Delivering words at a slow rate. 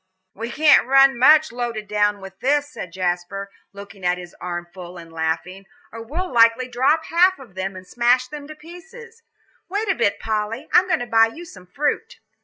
No: average, 190 wpm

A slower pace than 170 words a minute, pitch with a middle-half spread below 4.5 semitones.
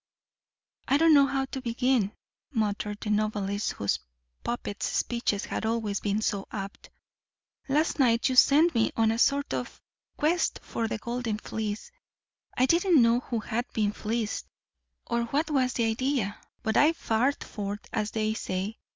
Yes: average, 160 wpm; average, 4.0 semitones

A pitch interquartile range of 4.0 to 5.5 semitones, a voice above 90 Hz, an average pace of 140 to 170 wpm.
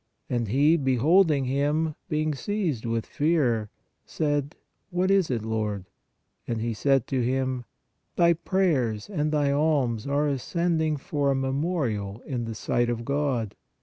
Yes: average, 4.8 semitones; medium, 140 Hz; average, 145 wpm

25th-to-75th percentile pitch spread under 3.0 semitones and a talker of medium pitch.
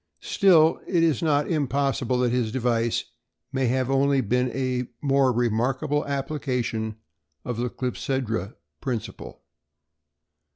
No: narrow, 2.6 semitones; low, 130 Hz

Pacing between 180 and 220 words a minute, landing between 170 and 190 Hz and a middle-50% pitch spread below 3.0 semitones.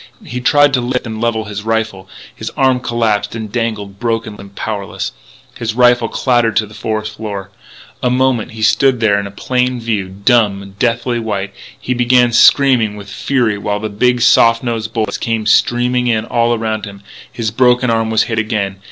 No: average, 185 wpm; low, 115 Hz; narrow, 2.5 semitones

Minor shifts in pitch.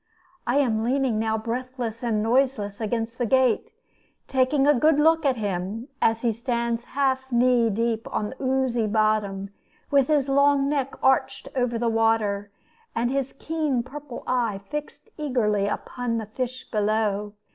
No: average, 3.3 semitones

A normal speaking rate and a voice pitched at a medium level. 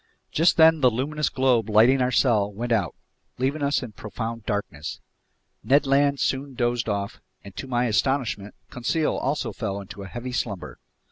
No: average, 165 wpm; low, 120 Hz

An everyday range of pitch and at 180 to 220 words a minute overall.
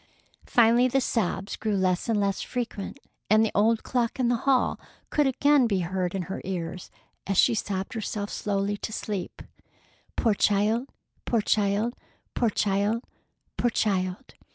No: average, 3.2 semitones; average, 155 wpm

